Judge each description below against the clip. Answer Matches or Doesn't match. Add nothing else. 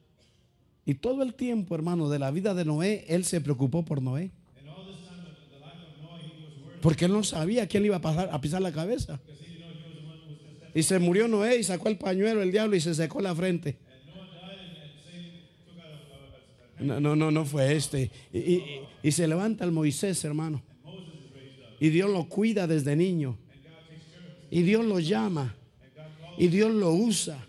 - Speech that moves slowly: Doesn't match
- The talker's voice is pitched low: Doesn't match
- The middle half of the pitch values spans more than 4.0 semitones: Doesn't match